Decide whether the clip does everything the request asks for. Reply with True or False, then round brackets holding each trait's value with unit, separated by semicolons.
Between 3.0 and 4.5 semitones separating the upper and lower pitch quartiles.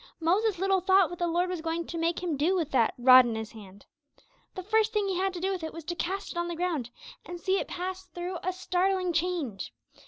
False (2.5 semitones)